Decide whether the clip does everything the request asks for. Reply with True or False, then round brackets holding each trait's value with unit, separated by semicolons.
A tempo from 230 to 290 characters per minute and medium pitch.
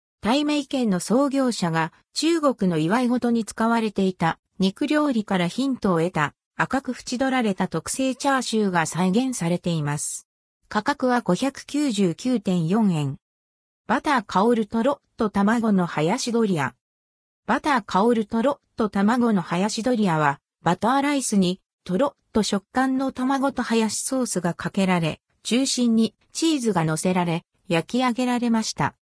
False (285 characters per minute; 220 Hz)